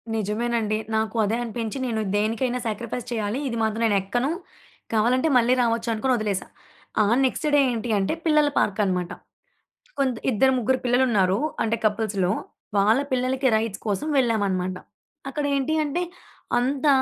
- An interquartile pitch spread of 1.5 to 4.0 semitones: Yes, average, 3.4 semitones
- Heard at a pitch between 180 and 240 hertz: Yes, high, 230 Hz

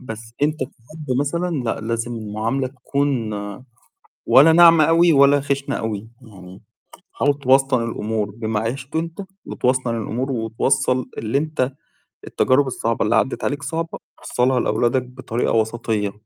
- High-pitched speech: No, low, 130 Hz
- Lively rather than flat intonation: No, average, 4.0 semitones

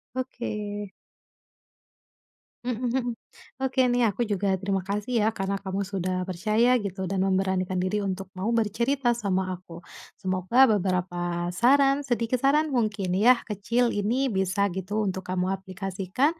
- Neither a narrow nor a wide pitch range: Yes, average, 4.2 semitones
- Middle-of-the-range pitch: No, high, 200 Hz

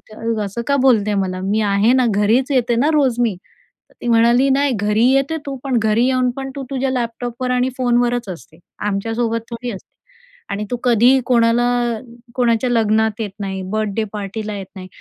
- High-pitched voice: Yes, high, 230 Hz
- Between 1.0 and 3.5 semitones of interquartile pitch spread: Yes, average, 3.0 semitones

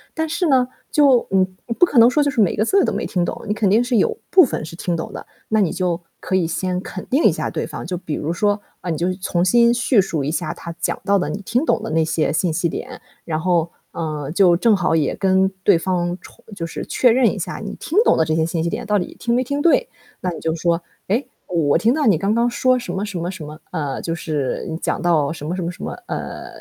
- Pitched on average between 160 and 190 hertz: Yes, medium, 185 Hz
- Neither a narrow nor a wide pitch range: No, wide, 5.9 semitones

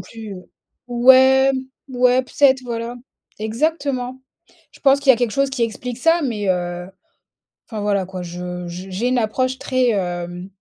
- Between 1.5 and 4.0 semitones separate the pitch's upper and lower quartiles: No, wide, 5.5 semitones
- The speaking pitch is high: Yes, high, 235 Hz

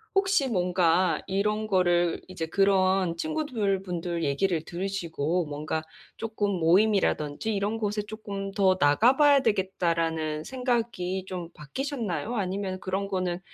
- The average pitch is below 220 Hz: Yes, high, 190 Hz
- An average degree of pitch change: Yes, average, 3.7 semitones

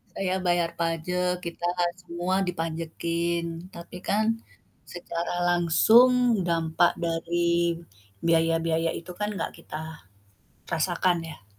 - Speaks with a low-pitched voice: No, medium, 170 Hz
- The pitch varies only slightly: Yes, narrow, 1.4 semitones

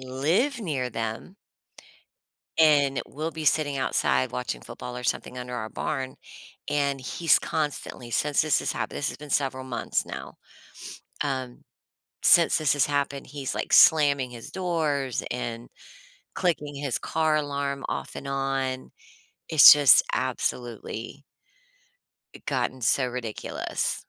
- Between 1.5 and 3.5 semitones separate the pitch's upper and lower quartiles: Yes, average, 2.9 semitones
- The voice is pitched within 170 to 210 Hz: No, medium, 140 Hz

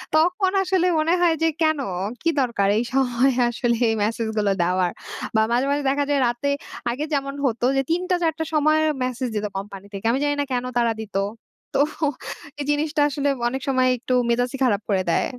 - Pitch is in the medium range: No, very high, 260 Hz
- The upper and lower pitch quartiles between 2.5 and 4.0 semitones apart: No, average, 4.4 semitones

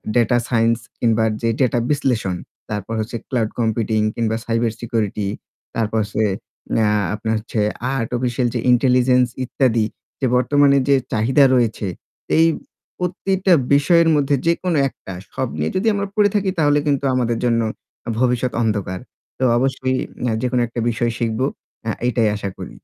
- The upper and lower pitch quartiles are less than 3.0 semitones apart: No, average, 3.4 semitones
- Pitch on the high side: No, low, 120 Hz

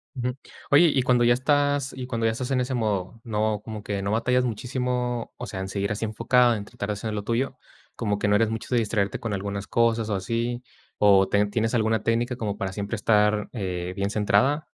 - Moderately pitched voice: No, low, 110 Hz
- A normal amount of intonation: Yes, average, 3.1 semitones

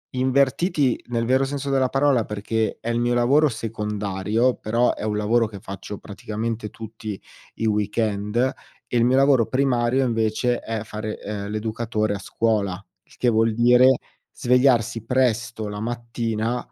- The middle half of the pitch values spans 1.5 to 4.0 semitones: Yes, narrow, 2.6 semitones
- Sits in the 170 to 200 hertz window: No, low, 115 Hz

